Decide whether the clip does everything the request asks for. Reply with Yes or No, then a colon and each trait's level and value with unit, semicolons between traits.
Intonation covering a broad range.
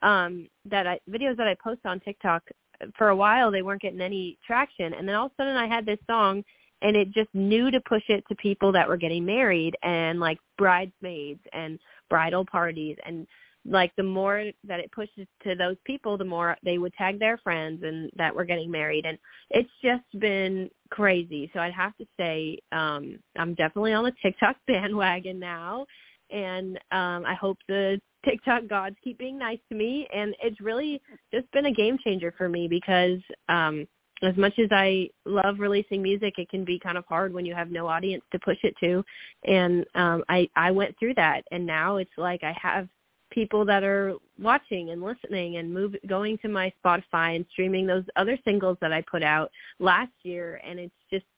No: average, 3.2 semitones